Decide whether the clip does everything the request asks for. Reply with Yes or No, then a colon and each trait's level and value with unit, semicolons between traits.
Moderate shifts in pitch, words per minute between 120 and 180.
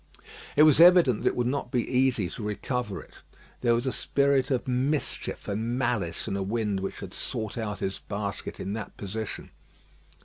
No: average, 4.1 semitones; average, 190 wpm